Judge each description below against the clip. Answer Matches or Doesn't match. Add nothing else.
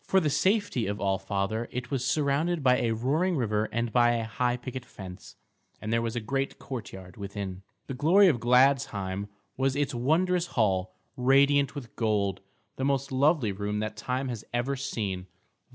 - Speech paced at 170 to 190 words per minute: Matches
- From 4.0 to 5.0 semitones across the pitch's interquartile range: Matches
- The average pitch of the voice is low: Matches